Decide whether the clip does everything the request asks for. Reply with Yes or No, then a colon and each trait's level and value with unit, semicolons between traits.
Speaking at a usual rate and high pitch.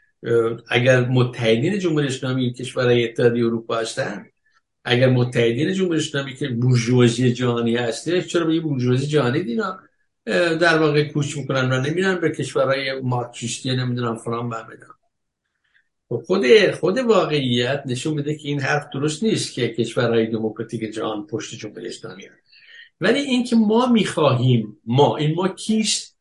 No: average, 135 wpm; low, 130 Hz